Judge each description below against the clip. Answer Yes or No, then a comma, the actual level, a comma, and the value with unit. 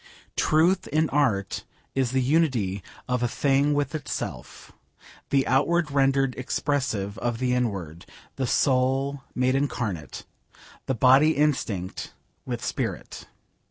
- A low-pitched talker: Yes, low, 130 Hz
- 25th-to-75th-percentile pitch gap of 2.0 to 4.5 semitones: Yes, average, 3.2 semitones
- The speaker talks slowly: Yes, slow, 120 wpm